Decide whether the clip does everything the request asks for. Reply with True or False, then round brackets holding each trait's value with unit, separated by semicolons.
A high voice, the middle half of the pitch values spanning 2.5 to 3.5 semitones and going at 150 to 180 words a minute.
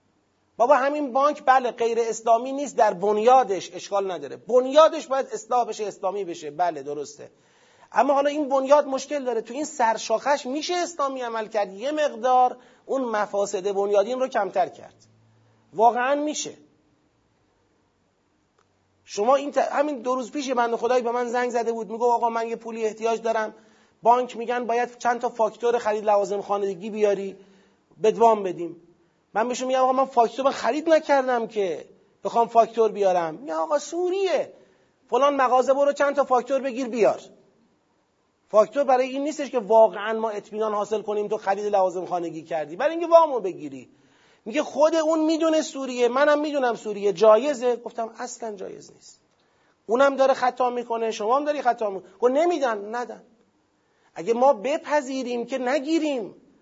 False (240 Hz; 4.4 semitones; 155 wpm)